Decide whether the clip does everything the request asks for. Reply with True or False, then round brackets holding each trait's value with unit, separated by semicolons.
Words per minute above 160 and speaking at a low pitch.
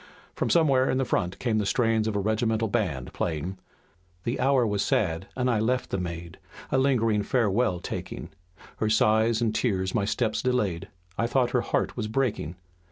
True (170 wpm; 110 Hz)